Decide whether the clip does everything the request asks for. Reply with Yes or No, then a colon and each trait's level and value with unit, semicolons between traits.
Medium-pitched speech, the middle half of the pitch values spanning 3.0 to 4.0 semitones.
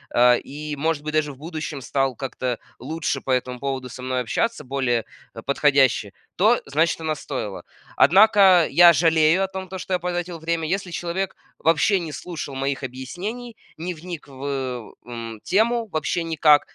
No: medium, 155 Hz; average, 4.8 semitones